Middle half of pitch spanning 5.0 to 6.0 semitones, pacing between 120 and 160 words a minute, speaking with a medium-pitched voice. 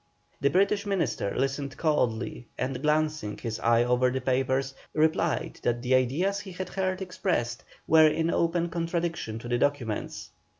Yes: wide, 5.4 semitones; average, 155 wpm; medium, 145 Hz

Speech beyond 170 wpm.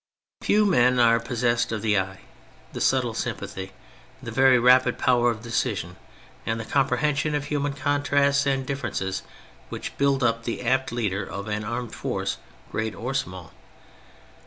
No: average, 155 wpm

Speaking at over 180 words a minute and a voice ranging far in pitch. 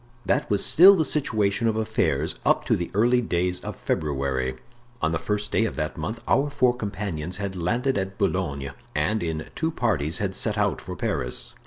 Yes: average, 190 wpm; wide, 6.3 semitones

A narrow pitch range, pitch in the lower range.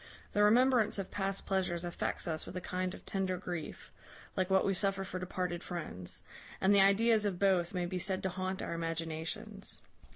No: narrow, 2.1 semitones; medium, 185 Hz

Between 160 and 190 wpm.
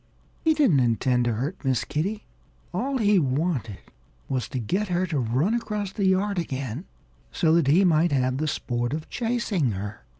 Yes: average, 175 wpm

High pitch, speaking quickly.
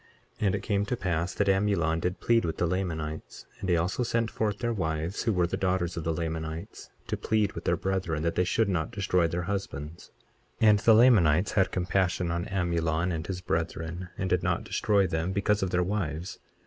No: very low, 90 Hz; fast, 210 wpm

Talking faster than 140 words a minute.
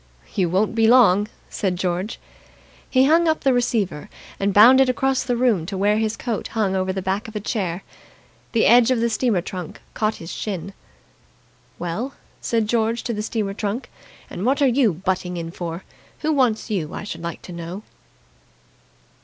Yes: average, 180 wpm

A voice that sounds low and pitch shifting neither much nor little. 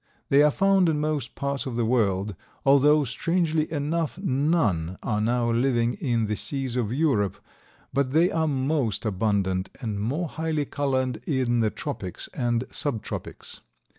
Yes: low, 130 Hz; average, 5.0 semitones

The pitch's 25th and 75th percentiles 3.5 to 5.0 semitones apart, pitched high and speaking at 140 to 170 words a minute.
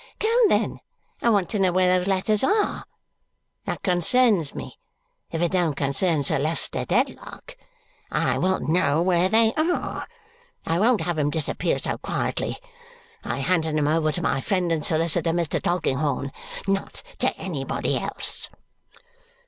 No: average, 3.9 semitones; medium, 175 Hz; average, 150 wpm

